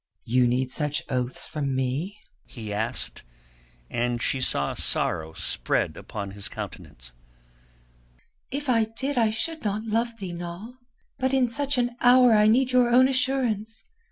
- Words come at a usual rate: Yes, average, 150 wpm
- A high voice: Yes, high, 215 Hz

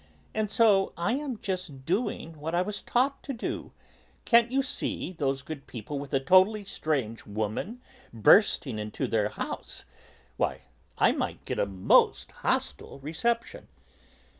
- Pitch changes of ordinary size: No, wide, 8.6 semitones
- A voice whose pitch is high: No, medium, 175 Hz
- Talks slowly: No, average, 145 wpm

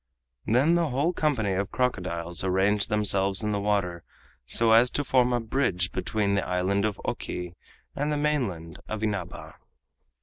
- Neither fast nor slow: Yes, average, 160 wpm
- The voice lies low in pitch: Yes, low, 105 Hz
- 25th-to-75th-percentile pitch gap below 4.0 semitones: No, average, 5.0 semitones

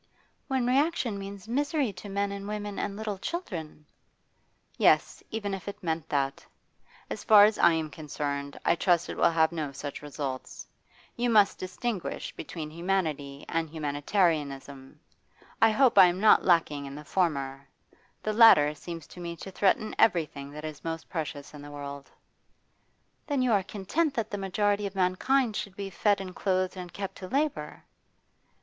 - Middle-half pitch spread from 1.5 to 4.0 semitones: No, wide, 5.5 semitones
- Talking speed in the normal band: Yes, average, 170 wpm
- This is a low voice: No, medium, 185 Hz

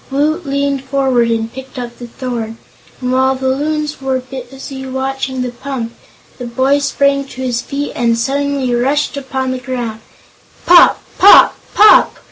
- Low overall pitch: No, very high, 265 Hz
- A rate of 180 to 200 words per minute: No, average, 155 wpm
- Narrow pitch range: Yes, narrow, 2.1 semitones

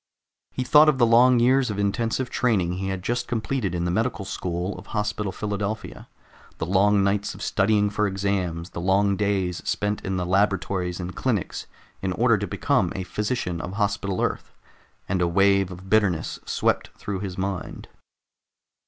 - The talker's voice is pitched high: No, low, 100 Hz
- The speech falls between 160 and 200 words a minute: Yes, average, 170 wpm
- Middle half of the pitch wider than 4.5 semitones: No, narrow, 2.4 semitones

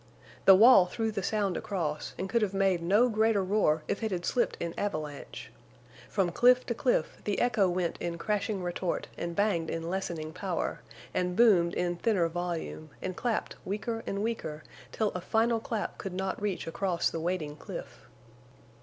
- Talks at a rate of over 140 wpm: Yes, average, 175 wpm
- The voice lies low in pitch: No, high, 190 Hz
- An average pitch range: Yes, average, 4.0 semitones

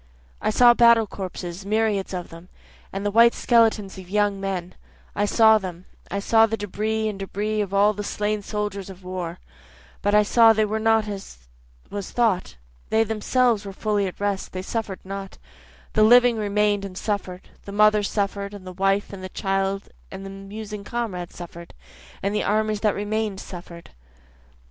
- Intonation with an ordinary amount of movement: No, narrow, 1.9 semitones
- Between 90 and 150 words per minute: No, average, 180 wpm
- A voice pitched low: No, high, 205 Hz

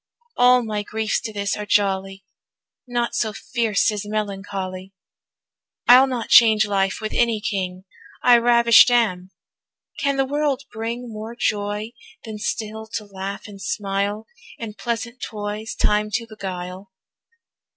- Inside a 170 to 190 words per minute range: No, slow, 135 wpm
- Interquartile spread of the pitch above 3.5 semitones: No, average, 2.8 semitones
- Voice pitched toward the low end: No, high, 215 Hz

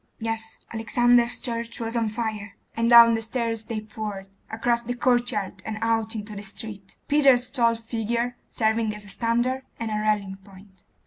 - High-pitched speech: Yes, high, 225 Hz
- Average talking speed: Yes, average, 170 wpm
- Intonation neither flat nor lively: No, narrow, 1.8 semitones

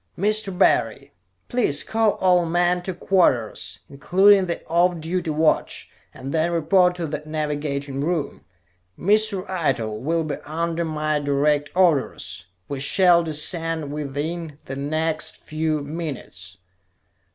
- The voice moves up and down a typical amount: Yes, average, 3.4 semitones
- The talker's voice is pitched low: No, medium, 160 Hz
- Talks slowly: Yes, slow, 125 wpm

